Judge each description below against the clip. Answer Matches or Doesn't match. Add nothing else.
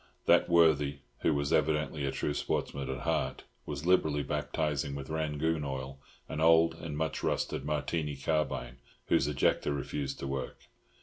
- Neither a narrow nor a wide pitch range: Doesn't match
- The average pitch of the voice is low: Matches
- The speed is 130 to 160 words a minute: Matches